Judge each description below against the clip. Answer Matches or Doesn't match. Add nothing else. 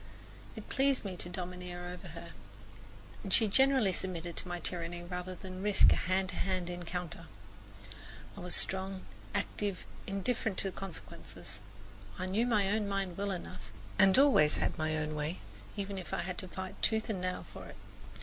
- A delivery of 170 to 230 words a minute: Matches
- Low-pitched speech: Doesn't match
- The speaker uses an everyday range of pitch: Doesn't match